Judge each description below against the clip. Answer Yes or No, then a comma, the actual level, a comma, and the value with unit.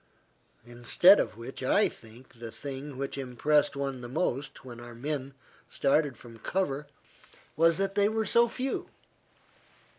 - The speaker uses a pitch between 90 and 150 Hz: Yes, low, 135 Hz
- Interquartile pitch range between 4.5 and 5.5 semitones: Yes, average, 5.1 semitones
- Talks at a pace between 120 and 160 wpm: Yes, average, 145 wpm